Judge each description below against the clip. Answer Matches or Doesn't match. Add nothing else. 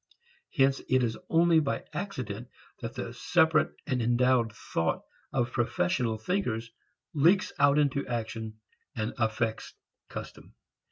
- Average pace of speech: Doesn't match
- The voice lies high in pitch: Doesn't match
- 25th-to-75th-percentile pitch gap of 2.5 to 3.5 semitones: Doesn't match